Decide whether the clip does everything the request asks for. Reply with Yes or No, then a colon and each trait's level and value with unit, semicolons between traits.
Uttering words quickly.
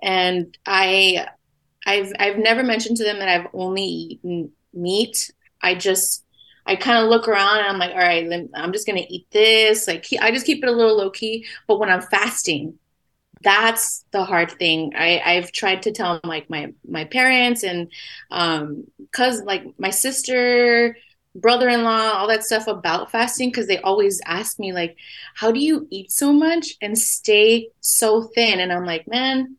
No: average, 180 wpm